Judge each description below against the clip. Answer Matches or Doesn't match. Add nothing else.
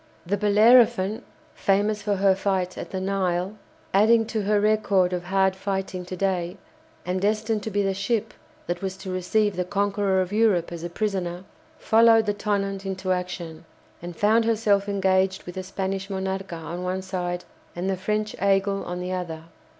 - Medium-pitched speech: Doesn't match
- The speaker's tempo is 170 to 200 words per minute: Matches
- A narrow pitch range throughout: Matches